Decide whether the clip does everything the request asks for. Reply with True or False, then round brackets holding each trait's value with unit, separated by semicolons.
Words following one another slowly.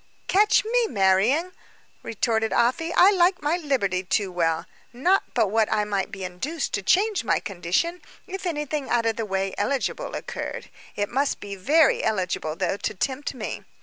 False (170 wpm)